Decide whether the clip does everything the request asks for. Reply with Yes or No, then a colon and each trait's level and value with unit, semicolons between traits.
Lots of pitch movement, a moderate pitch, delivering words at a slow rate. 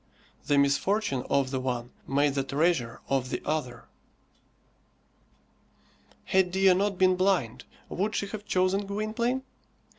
Yes: wide, 6.6 semitones; medium, 175 Hz; slow, 125 wpm